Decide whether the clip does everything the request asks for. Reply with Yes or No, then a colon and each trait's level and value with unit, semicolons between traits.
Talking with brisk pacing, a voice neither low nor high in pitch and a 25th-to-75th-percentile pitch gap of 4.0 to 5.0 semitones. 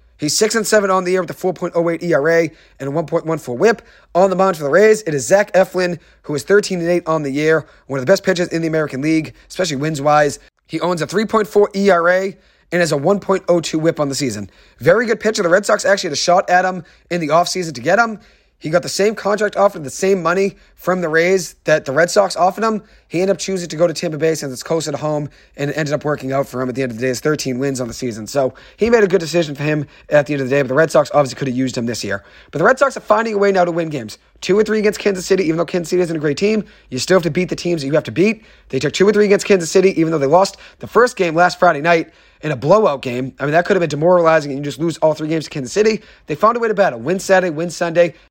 Yes: fast, 300 wpm; medium, 170 Hz; average, 4.4 semitones